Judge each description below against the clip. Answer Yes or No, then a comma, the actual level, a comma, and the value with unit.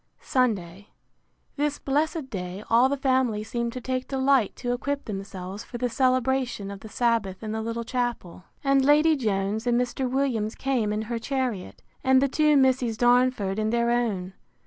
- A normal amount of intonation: Yes, average, 3.7 semitones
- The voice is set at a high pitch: Yes, high, 240 Hz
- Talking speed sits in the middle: Yes, average, 170 wpm